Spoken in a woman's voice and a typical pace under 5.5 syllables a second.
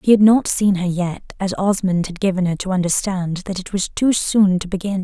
Yes: female; 5.1 syllables/s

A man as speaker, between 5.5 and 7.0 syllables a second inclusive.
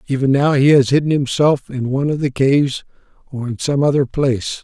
Yes: male; 5.7 syllables/s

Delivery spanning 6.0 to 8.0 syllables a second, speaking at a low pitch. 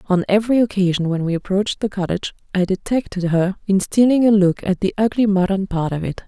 No: 6.1 syllables/s; high, 195 Hz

